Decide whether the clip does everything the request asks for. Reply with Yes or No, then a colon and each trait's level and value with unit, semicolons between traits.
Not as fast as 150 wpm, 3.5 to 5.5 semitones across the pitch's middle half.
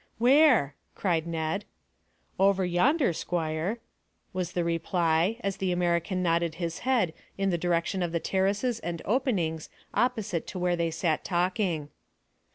No: average, 140 wpm; average, 3.0 semitones